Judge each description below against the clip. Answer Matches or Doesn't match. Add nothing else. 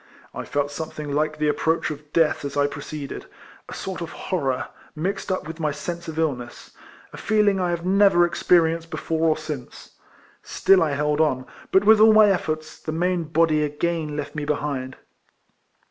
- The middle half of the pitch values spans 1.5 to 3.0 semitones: Matches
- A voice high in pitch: Doesn't match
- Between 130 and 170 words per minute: Doesn't match